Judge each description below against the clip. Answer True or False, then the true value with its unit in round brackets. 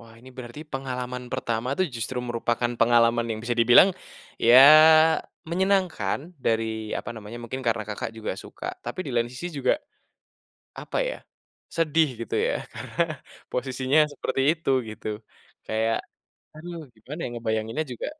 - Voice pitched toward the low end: True (120 Hz)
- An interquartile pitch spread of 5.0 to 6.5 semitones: False (3.2 semitones)